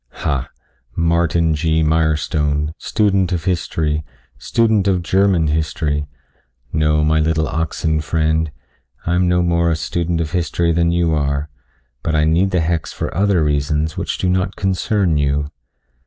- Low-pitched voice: Yes, very low, 80 Hz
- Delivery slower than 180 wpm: Yes, average, 150 wpm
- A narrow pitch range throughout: Yes, narrow, 2.3 semitones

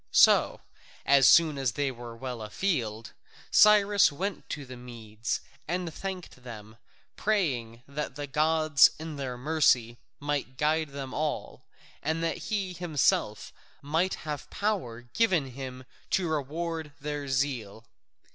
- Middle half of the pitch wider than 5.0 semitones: No, average, 4.7 semitones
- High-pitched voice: No, medium, 145 Hz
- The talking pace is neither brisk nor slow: No, slow, 130 wpm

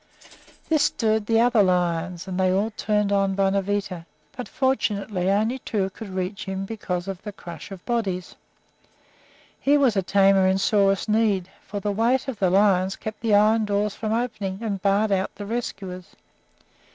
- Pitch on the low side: No, high, 200 Hz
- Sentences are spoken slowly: No, average, 165 wpm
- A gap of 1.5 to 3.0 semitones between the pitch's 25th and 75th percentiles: Yes, narrow, 2.4 semitones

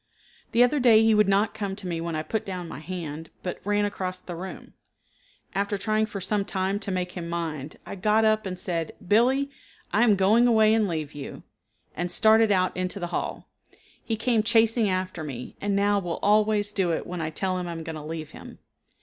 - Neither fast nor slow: No, fast, 220 wpm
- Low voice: No, high, 195 Hz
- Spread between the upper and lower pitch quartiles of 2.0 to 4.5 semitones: Yes, average, 3.7 semitones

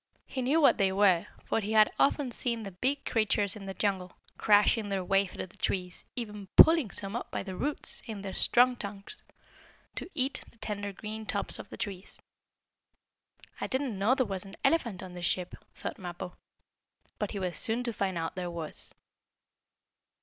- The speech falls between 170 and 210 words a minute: Yes, average, 185 wpm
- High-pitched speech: Yes, high, 205 Hz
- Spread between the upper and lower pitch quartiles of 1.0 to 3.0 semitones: No, average, 3.8 semitones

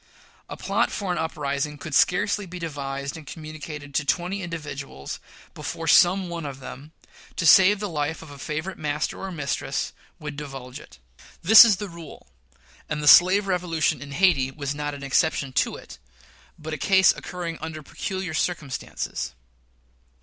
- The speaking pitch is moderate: Yes, medium, 155 Hz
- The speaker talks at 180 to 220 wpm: No, average, 165 wpm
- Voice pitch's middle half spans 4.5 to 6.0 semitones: No, average, 3.8 semitones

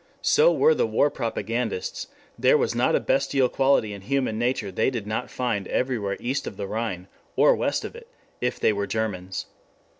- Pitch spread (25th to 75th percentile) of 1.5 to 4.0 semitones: No, wide, 5.6 semitones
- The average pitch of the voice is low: Yes, low, 120 Hz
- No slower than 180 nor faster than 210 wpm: Yes, average, 185 wpm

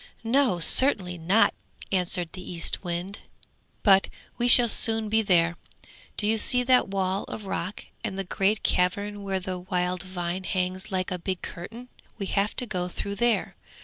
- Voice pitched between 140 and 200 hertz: Yes, high, 190 Hz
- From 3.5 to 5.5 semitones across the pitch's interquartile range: No, average, 3.1 semitones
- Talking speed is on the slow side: No, average, 165 wpm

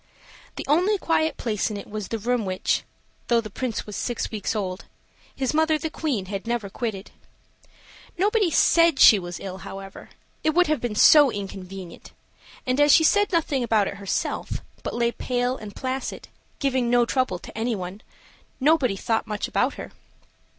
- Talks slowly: No, average, 170 wpm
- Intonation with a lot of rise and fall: Yes, wide, 6.4 semitones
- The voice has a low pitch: No, high, 235 Hz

